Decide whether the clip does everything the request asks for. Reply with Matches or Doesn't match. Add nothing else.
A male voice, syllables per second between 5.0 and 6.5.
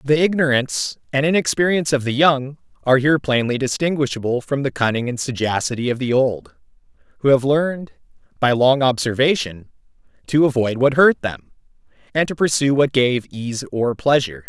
Matches